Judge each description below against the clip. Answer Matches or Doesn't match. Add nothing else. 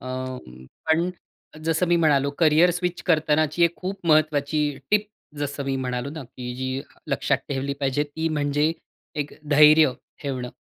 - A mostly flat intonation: Doesn't match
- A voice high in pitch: Doesn't match